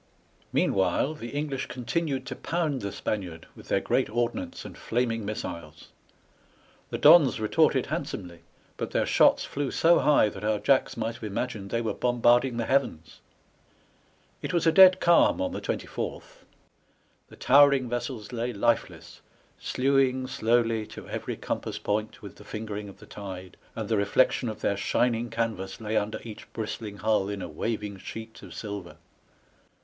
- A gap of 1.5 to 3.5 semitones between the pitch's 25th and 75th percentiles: No, average, 4.2 semitones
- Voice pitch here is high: No, low, 115 Hz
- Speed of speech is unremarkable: Yes, average, 160 wpm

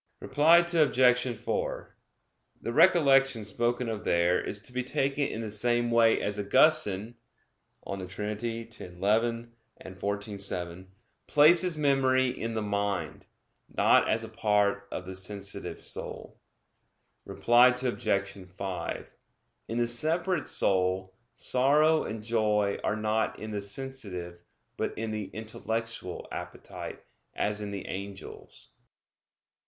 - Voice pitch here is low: Yes, low, 110 Hz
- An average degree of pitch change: Yes, average, 4.1 semitones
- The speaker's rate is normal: No, slow, 125 wpm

